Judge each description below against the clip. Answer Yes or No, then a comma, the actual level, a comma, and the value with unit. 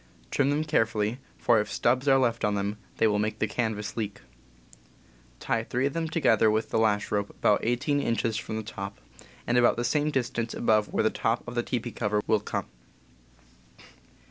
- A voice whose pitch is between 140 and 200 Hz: No, low, 115 Hz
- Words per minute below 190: No, average, 195 wpm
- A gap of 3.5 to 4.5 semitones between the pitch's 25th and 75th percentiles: No, narrow, 2.5 semitones